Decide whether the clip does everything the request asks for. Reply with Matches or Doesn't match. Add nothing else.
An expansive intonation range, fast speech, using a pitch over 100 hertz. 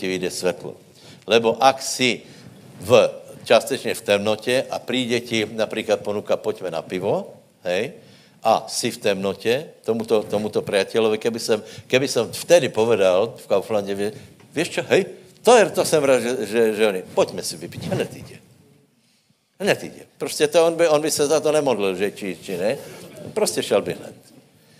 Matches